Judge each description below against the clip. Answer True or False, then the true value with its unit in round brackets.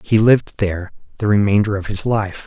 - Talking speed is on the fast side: False (195 wpm)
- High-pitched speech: False (105 Hz)